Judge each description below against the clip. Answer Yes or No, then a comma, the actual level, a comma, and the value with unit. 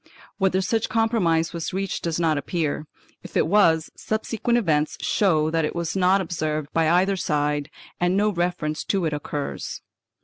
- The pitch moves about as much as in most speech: Yes, average, 3.8 semitones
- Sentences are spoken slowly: No, average, 165 wpm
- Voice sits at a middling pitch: Yes, medium, 170 Hz